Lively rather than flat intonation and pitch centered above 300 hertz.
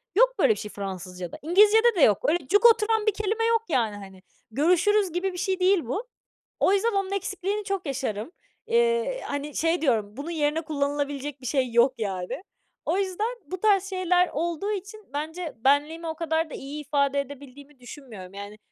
Yes: wide, 6.6 semitones; very high, 320 Hz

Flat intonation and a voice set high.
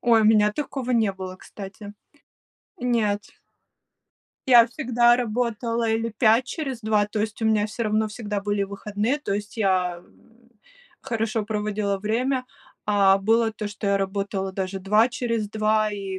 Yes: narrow, 2.3 semitones; high, 215 Hz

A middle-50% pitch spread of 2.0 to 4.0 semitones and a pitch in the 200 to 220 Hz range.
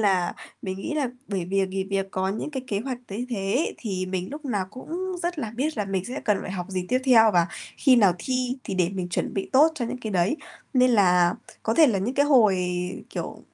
No: average, 5.2 semitones; high, 210 Hz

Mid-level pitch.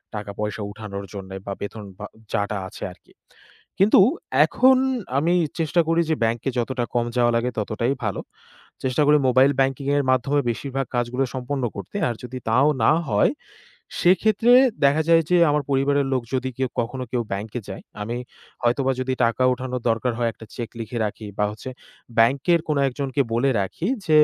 No: low, 125 Hz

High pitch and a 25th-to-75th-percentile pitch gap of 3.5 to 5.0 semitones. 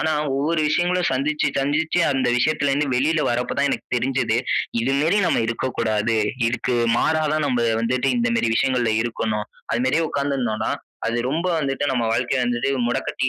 No: low, 135 Hz; average, 4.2 semitones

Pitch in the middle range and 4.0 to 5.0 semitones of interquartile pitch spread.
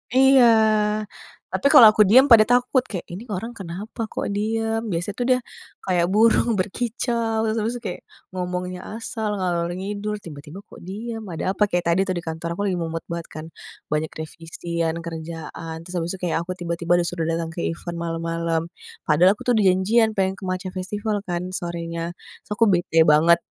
Yes: medium, 180 Hz; average, 4.4 semitones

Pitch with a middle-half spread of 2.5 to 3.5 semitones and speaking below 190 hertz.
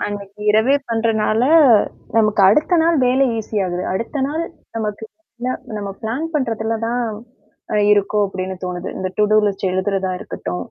No: average, 2.9 semitones; high, 215 Hz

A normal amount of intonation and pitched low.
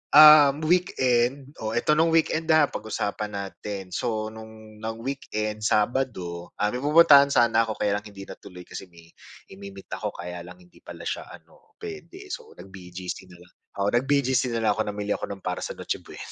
No: wide, 5.9 semitones; low, 110 Hz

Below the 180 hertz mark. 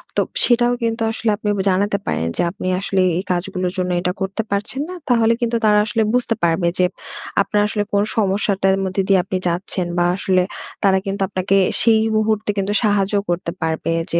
No: high, 195 Hz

